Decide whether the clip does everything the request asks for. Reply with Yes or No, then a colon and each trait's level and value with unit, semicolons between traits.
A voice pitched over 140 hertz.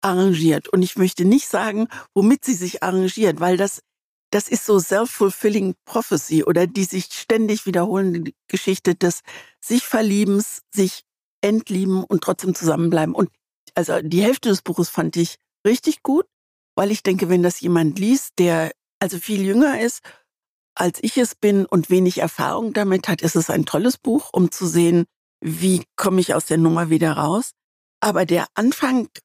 Yes: high, 190 Hz